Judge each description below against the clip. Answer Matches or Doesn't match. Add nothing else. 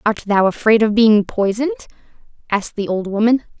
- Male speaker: Doesn't match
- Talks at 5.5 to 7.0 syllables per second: Matches